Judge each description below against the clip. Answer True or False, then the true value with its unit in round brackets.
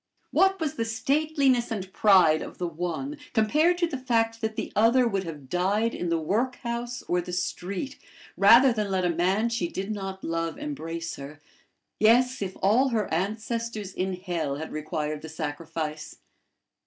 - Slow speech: False (165 wpm)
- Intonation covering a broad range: True (5.9 semitones)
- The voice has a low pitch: False (200 Hz)